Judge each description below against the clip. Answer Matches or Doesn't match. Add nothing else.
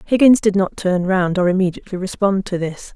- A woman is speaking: Matches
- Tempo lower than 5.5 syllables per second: Doesn't match